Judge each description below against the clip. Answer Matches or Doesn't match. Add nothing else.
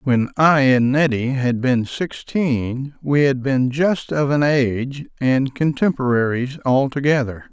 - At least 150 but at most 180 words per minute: Doesn't match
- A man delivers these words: Matches